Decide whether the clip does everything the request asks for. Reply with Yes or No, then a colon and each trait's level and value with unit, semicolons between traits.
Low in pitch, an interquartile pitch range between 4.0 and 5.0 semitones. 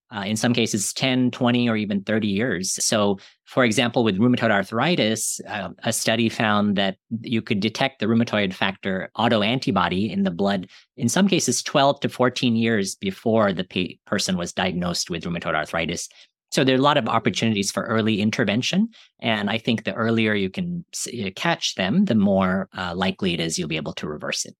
No: low, 115 Hz; average, 3.4 semitones